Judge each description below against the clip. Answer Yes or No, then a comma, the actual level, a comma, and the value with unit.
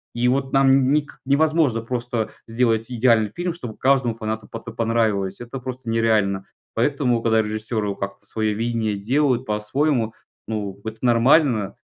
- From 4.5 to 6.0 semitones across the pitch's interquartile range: No, average, 3.1 semitones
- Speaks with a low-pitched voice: Yes, low, 115 Hz